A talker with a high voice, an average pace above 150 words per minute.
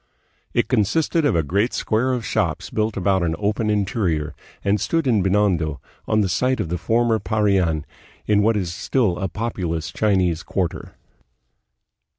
No: low, 100 Hz; average, 160 wpm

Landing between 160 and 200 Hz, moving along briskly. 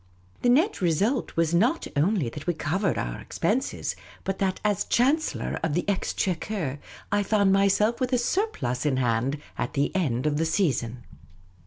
No: medium, 185 Hz; average, 170 wpm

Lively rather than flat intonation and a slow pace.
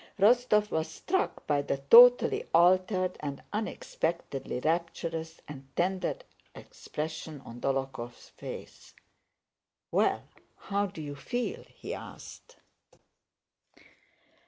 Yes: wide, 6.1 semitones; slow, 95 wpm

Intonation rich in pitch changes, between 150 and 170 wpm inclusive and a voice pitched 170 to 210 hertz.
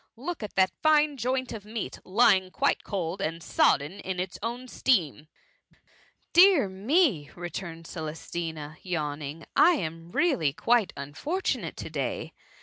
No: wide, 7.5 semitones; average, 140 wpm; high, 190 Hz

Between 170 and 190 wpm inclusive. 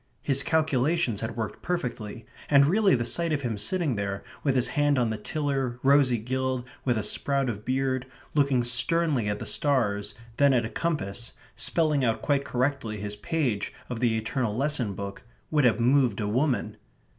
Yes: average, 180 wpm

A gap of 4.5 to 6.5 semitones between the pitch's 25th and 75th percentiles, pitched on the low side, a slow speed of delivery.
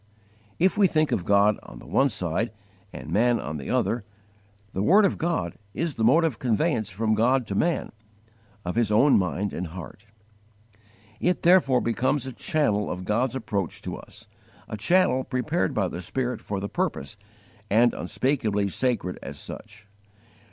No: average, 5.0 semitones; low, 115 Hz; average, 165 wpm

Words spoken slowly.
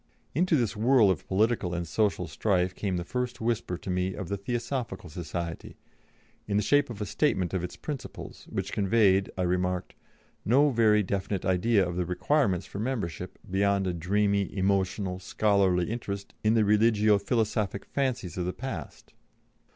No: average, 165 wpm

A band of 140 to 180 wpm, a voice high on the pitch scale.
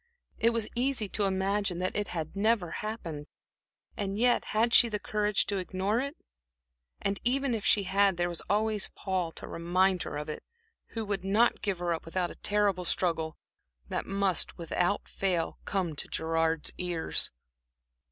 Yes: average, 170 wpm; high, 195 Hz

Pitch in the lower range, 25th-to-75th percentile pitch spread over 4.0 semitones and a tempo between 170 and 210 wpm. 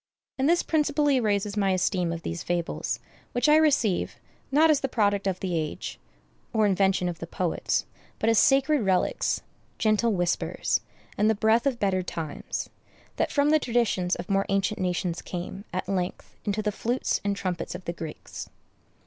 No: high, 200 Hz; average, 4.9 semitones; average, 175 wpm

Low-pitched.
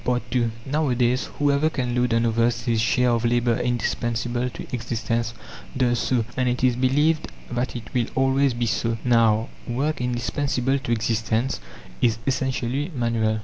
Yes: low, 120 Hz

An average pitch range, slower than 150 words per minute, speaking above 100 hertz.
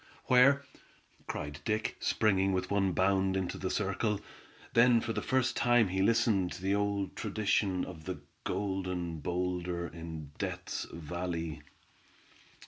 No: average, 3.1 semitones; slow, 135 wpm; very low, 95 Hz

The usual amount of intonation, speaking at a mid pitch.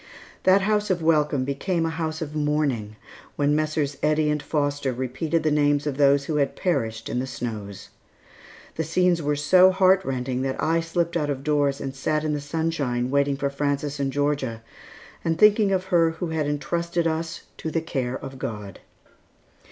Yes: average, 3.1 semitones; medium, 150 Hz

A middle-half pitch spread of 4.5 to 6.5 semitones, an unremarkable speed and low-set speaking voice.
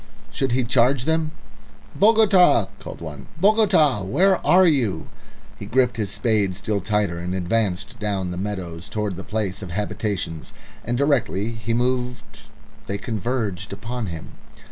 Yes: average, 5.1 semitones; average, 145 wpm; low, 110 Hz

